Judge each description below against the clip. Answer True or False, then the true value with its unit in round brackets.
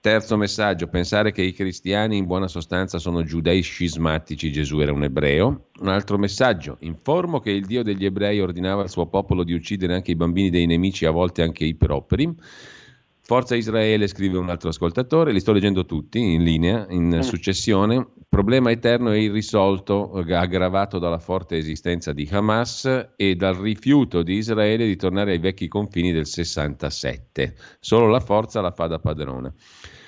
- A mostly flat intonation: False (3.6 semitones)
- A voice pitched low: True (95 Hz)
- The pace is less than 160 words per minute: False (170 wpm)